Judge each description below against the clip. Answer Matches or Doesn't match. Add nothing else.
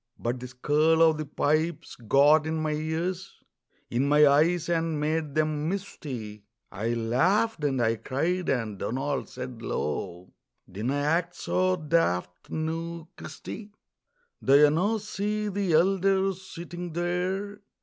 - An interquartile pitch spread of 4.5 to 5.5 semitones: Matches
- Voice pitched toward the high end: Doesn't match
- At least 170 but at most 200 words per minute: Doesn't match